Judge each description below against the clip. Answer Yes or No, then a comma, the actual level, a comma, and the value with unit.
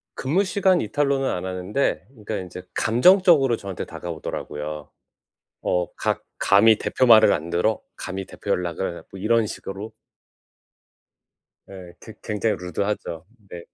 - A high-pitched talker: No, low, 100 Hz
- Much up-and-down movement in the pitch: No, average, 4.6 semitones